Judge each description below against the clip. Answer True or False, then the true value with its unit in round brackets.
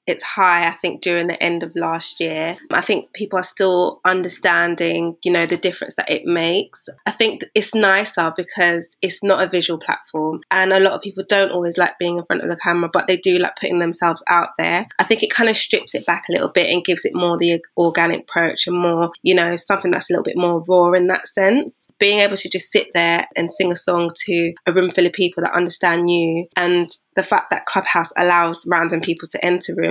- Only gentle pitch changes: True (1.6 semitones)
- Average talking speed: False (235 wpm)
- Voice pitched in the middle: True (175 Hz)